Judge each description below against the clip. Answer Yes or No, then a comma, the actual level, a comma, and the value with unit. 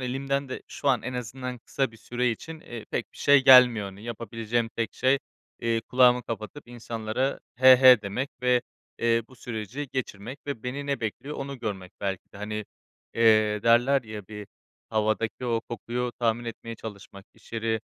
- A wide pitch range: No, average, 2.8 semitones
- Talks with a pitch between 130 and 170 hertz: No, low, 120 Hz